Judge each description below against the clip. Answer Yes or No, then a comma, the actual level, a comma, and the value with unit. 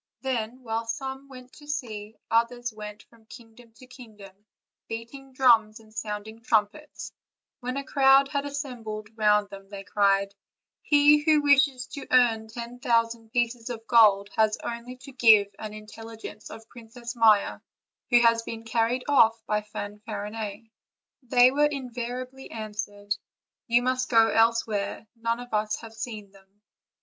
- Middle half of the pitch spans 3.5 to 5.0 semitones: No, average, 2.8 semitones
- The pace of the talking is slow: No, average, 150 wpm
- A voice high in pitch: Yes, high, 230 Hz